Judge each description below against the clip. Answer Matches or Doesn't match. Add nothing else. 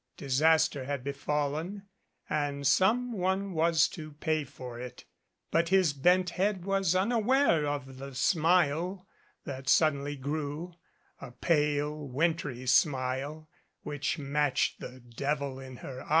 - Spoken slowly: Matches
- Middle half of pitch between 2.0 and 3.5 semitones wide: Doesn't match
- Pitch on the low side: Doesn't match